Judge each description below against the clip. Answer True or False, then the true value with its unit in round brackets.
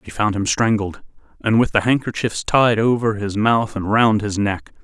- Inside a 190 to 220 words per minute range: True (200 wpm)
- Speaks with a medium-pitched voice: False (110 Hz)